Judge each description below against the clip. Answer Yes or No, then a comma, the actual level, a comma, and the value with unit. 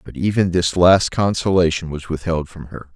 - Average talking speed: Yes, average, 185 wpm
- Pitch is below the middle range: Yes, very low, 85 Hz